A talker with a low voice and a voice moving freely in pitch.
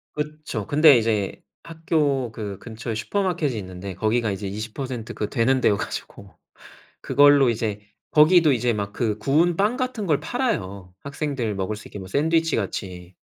Yes: low, 120 Hz; wide, 6.5 semitones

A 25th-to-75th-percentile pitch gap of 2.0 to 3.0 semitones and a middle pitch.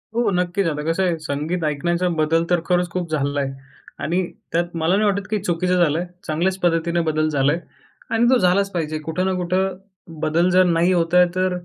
Yes: narrow, 2.4 semitones; medium, 175 Hz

